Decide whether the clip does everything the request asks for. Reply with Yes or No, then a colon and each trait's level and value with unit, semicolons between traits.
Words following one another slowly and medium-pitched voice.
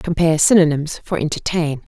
Yes: slow, 125 wpm; medium, 160 Hz